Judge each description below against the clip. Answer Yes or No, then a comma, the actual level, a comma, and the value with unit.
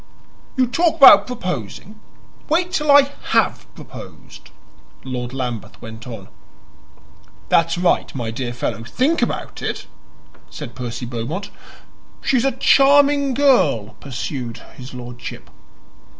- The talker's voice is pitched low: No, medium, 150 Hz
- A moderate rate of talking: No, slow, 115 wpm